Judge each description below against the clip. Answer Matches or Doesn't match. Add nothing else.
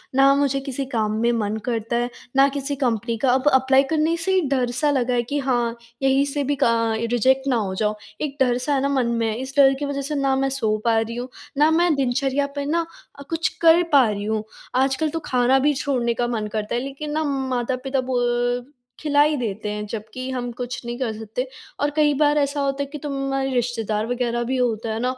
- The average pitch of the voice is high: Matches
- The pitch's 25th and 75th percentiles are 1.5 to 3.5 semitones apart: Matches